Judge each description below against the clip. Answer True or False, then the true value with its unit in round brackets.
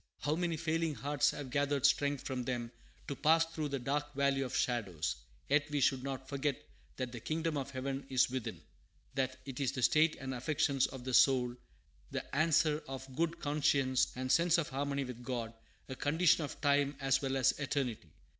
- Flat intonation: True (2.3 semitones)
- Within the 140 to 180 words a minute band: False (195 wpm)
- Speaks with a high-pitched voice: False (140 Hz)